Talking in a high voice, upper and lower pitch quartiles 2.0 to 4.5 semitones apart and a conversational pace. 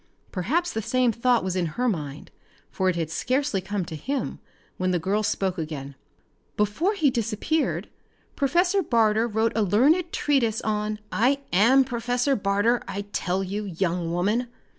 No: high, 215 Hz; average, 5.3 semitones; average, 160 wpm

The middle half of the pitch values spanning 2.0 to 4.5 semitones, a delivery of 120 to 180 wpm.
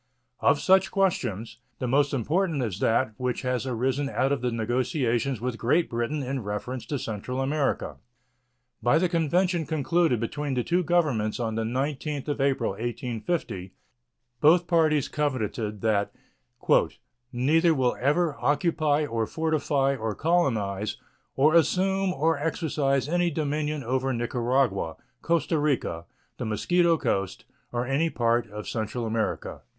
No: average, 5.1 semitones; slow, 135 wpm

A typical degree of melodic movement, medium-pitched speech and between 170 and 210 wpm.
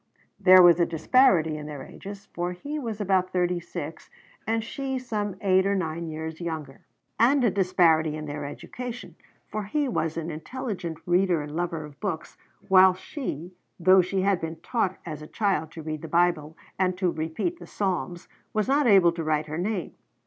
Yes: average, 4.1 semitones; medium, 180 Hz; average, 185 wpm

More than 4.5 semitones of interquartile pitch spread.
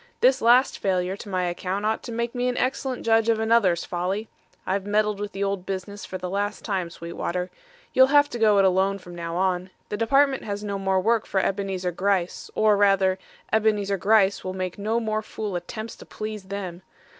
No: average, 2.9 semitones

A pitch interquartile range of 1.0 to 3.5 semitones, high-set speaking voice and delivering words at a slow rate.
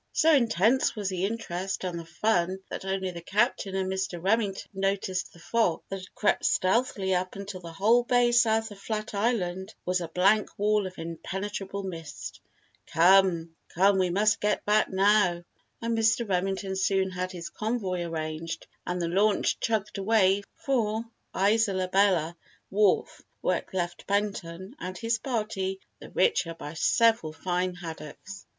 No: average, 2.9 semitones; high, 195 Hz; average, 155 wpm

